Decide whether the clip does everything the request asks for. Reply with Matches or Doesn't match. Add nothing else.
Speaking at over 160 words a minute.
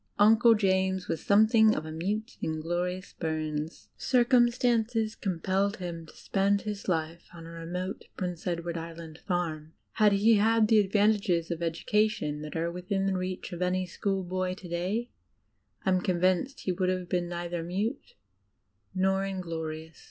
Doesn't match